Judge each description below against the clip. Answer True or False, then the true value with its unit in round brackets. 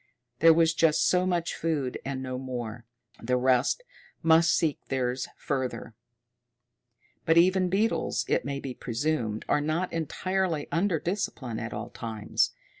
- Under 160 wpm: True (140 wpm)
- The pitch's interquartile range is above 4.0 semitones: True (4.9 semitones)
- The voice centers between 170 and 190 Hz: False (150 Hz)